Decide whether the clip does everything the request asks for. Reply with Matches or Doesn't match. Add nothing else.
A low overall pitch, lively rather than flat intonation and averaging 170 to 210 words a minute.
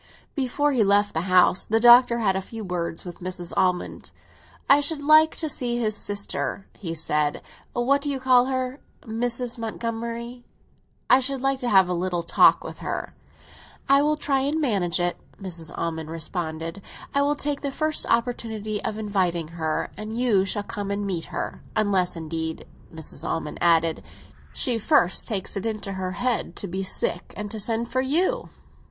Doesn't match